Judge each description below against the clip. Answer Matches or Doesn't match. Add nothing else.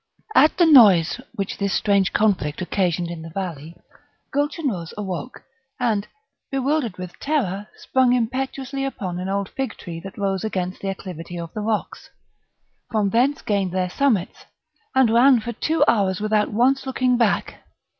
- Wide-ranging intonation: Matches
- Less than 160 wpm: Matches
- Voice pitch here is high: Matches